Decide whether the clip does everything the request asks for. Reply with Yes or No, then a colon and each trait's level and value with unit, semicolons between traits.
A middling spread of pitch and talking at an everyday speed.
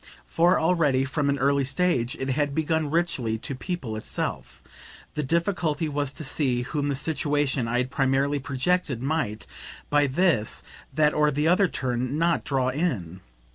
Yes: average, 3.5 semitones; average, 160 wpm